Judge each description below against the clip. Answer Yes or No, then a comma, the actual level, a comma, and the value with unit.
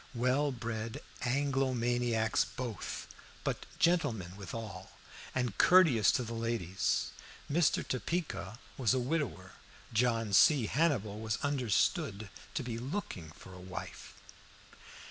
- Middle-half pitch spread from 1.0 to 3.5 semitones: No, average, 4.0 semitones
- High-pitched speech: No, low, 120 Hz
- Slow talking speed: Yes, slow, 115 wpm